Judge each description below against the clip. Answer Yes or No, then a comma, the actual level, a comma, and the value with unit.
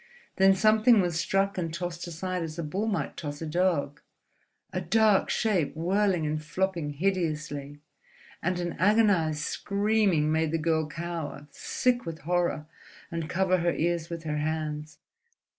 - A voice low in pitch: No, medium, 170 Hz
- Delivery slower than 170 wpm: Yes, average, 145 wpm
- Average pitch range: Yes, average, 3.6 semitones